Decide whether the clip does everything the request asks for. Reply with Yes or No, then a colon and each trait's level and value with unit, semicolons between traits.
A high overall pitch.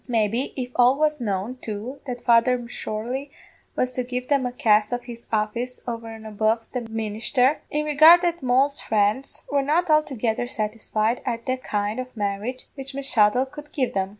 Yes: high, 245 Hz